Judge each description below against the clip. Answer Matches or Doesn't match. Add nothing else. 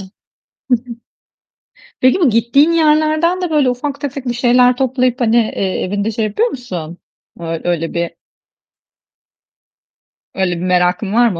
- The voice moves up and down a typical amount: Doesn't match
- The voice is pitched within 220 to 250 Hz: Matches